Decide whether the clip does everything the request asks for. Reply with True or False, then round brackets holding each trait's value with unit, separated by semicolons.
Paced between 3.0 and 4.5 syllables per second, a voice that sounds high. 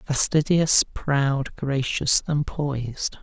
False (3.1 syllables/s; 140 Hz)